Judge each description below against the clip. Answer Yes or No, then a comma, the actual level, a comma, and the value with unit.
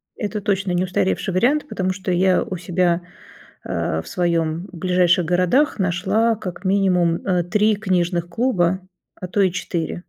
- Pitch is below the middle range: No, medium, 185 Hz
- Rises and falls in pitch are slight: Yes, narrow, 2.2 semitones